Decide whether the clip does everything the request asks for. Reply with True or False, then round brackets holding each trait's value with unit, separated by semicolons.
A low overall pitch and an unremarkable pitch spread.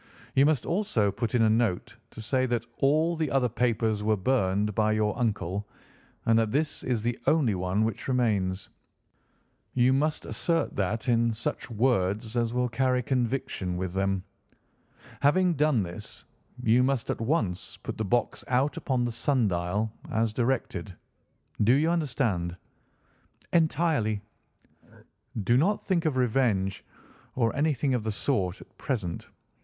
True (115 Hz; 4.3 semitones)